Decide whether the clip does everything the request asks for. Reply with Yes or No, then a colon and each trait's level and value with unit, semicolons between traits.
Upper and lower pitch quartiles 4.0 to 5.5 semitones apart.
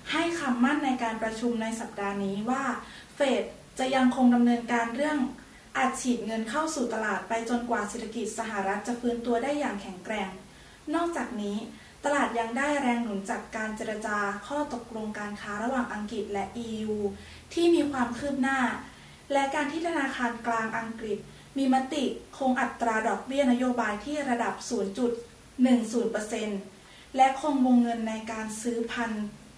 No: average, 3.3 semitones